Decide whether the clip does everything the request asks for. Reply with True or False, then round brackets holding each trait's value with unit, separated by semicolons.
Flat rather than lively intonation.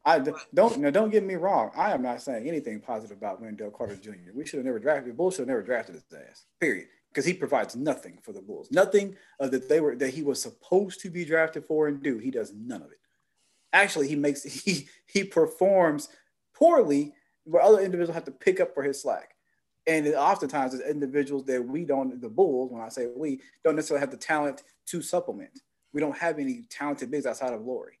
False (5.4 semitones)